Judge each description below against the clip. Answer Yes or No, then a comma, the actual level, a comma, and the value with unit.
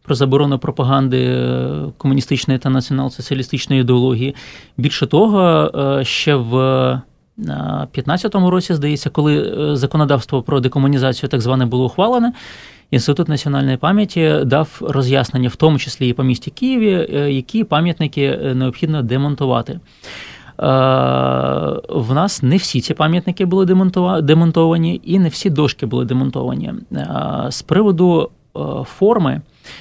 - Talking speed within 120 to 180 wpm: No, average, 110 wpm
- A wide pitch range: No, average, 3.8 semitones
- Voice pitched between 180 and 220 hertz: No, medium, 140 Hz